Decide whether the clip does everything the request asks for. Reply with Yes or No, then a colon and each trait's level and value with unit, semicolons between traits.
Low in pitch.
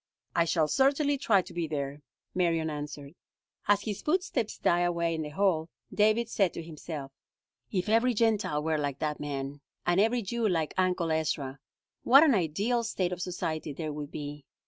No: medium, 170 Hz